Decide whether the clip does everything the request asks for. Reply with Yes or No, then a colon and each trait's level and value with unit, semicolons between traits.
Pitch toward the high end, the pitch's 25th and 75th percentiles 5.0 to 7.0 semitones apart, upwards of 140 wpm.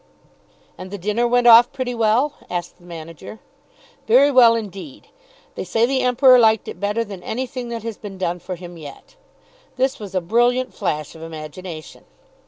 Yes: high, 220 Hz; wide, 5.4 semitones; average, 175 wpm